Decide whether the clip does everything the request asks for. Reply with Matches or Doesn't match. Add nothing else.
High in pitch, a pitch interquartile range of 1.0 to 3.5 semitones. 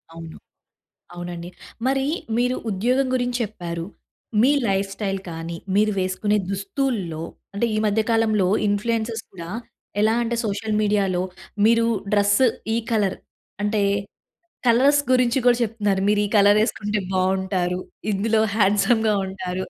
Matches